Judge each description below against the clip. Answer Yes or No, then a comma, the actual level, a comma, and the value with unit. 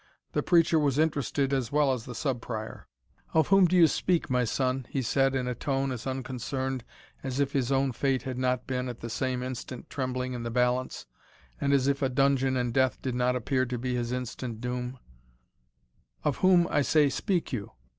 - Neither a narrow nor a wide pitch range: No, narrow, 1.9 semitones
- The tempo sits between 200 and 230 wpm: Yes, fast, 205 wpm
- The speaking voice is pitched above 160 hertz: No, low, 130 Hz